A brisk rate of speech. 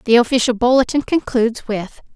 No: average, 140 wpm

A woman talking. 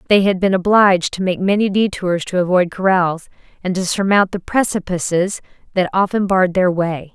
Yes: female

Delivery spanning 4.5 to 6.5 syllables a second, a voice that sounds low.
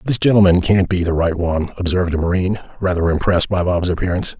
No: 7.0 syllables/s; very low, 90 Hz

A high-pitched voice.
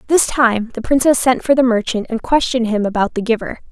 Yes: high, 235 Hz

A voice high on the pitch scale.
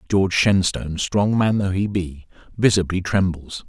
No: very low, 95 Hz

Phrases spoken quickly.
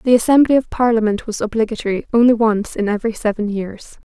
No: average, 175 wpm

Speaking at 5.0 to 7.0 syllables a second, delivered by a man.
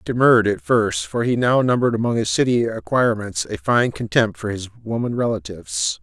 Yes: 5.7 syllables/s; male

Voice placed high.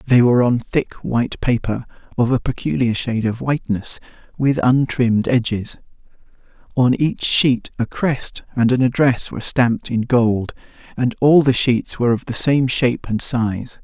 No: low, 120 Hz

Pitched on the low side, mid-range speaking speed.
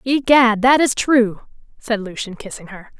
No: high, 230 Hz; average, 160 wpm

